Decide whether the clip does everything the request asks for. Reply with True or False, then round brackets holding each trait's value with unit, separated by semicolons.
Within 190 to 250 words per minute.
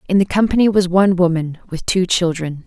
True (205 wpm)